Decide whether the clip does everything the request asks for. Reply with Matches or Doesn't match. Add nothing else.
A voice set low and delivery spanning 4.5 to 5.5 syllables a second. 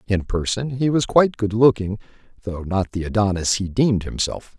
Matches